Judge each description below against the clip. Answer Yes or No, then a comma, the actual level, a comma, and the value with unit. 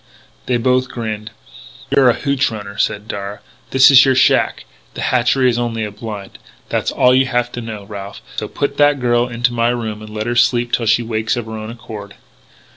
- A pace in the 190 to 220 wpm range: Yes, fast, 205 wpm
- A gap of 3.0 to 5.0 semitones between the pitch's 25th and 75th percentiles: No, narrow, 2.6 semitones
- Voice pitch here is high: No, low, 120 Hz